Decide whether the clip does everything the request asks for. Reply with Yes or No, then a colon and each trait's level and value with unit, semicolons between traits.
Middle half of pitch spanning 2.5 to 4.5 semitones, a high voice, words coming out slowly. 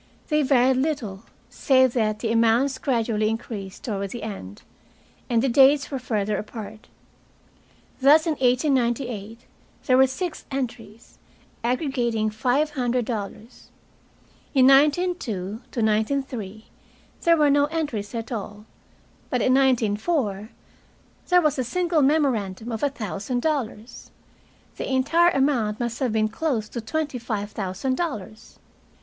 Yes: average, 4.2 semitones; high, 245 Hz; slow, 130 wpm